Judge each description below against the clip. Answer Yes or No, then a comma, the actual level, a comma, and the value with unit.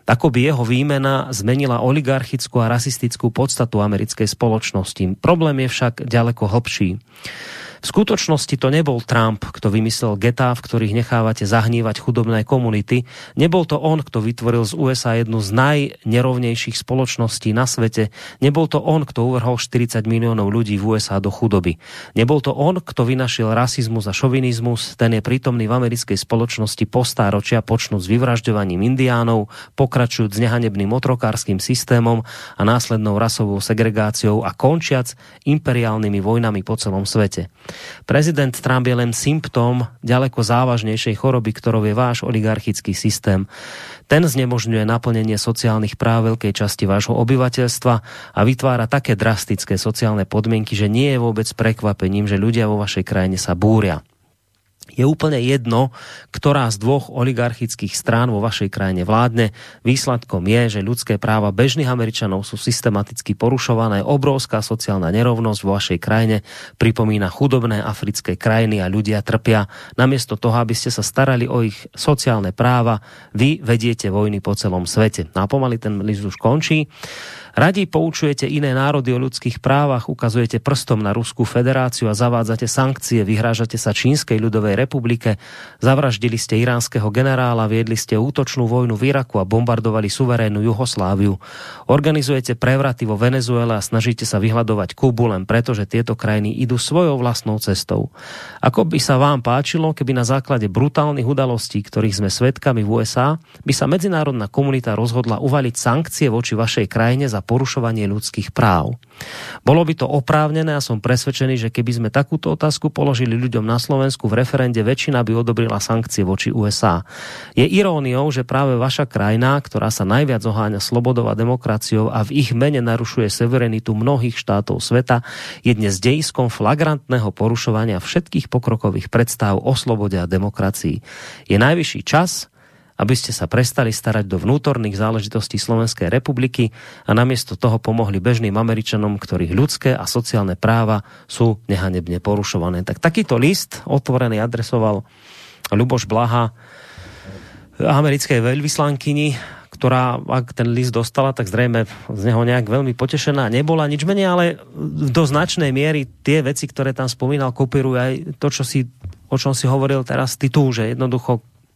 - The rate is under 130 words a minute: No, average, 145 wpm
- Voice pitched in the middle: No, low, 120 Hz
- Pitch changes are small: No, average, 3.2 semitones